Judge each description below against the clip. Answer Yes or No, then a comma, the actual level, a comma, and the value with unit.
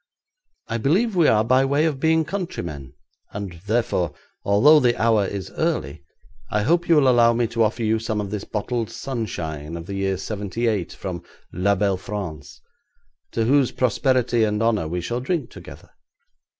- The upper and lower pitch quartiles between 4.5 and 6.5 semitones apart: Yes, average, 4.9 semitones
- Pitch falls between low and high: No, low, 110 Hz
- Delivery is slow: No, average, 170 wpm